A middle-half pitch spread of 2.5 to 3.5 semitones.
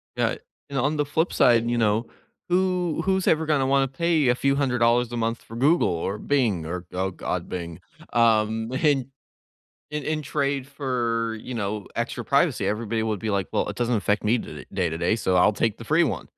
No: average, 4.7 semitones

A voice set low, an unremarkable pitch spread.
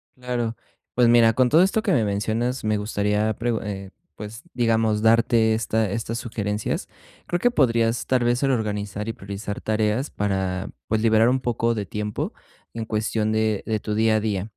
No: low, 110 Hz; narrow, 2.1 semitones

